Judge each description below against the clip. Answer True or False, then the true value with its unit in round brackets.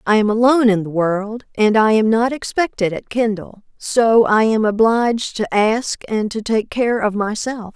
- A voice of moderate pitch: False (220 Hz)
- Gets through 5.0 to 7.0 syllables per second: False (4.4 syllables/s)